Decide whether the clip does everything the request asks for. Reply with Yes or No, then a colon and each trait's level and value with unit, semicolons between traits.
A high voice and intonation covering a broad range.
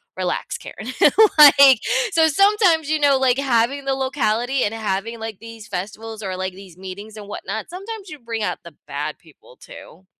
Yes: high, 230 Hz; wide, 5.8 semitones